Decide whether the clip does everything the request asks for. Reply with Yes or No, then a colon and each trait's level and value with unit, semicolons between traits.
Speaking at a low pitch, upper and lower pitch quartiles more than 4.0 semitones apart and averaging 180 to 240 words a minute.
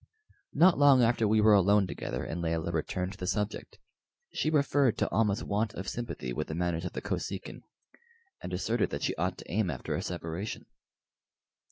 Yes: low, 100 Hz; average, 4.8 semitones; average, 185 wpm